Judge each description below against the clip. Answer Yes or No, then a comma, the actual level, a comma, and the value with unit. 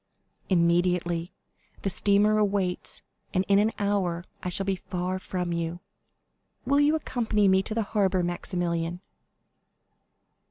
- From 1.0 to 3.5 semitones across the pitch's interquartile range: Yes, average, 2.7 semitones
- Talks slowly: Yes, slow, 125 wpm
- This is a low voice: No, medium, 185 Hz